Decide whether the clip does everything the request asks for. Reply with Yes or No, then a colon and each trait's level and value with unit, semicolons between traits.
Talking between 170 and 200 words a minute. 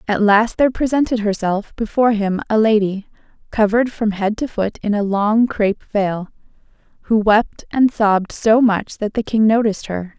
Yes: average, 175 wpm